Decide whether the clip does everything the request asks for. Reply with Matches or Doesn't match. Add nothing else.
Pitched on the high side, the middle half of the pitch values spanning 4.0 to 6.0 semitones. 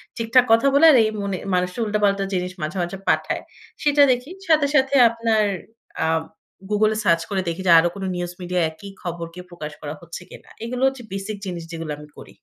Matches